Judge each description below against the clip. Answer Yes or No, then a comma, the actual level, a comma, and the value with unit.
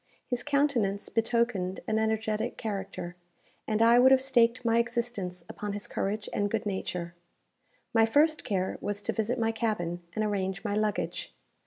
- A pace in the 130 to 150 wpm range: No, average, 160 wpm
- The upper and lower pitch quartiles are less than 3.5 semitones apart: Yes, average, 2.9 semitones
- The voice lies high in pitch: Yes, high, 220 Hz